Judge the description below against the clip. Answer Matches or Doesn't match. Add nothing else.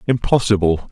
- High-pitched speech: Doesn't match